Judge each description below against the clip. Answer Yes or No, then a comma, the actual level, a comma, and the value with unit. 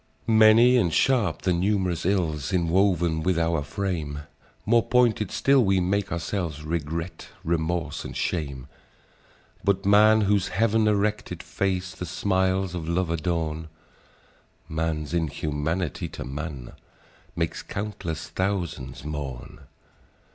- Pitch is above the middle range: No, very low, 90 Hz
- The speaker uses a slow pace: Yes, slow, 115 wpm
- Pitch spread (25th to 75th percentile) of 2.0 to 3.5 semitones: No, average, 4.0 semitones